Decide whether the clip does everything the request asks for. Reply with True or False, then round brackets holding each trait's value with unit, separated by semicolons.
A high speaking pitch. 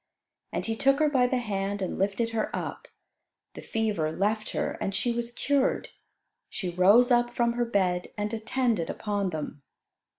True (220 Hz)